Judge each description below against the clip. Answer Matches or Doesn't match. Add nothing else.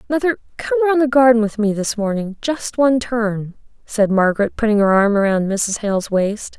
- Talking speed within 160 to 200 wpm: Matches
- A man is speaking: Doesn't match